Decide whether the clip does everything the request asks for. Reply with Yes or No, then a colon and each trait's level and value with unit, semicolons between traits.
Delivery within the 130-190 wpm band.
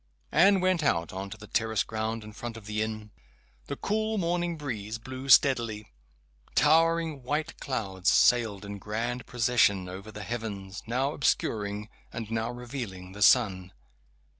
Yes: average, 150 wpm